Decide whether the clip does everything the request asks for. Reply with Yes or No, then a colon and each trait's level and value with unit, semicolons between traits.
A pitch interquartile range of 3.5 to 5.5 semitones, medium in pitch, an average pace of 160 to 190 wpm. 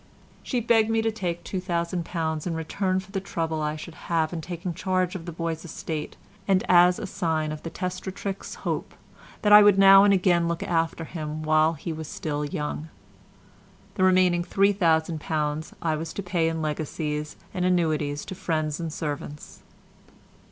No: average, 2.9 semitones; medium, 170 Hz; average, 170 wpm